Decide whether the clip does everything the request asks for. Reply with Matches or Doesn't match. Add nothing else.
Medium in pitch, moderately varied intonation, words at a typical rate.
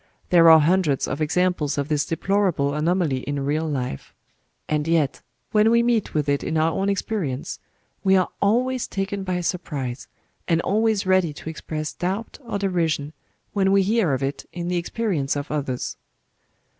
Matches